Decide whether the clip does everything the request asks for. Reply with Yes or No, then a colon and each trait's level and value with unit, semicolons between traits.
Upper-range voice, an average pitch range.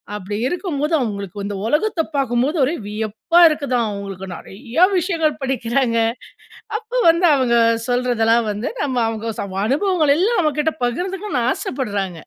No: very high, 255 Hz; wide, 6.2 semitones